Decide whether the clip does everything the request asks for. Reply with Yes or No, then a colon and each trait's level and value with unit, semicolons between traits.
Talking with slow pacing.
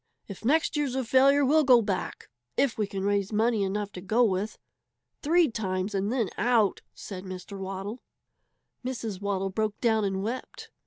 No: average, 170 wpm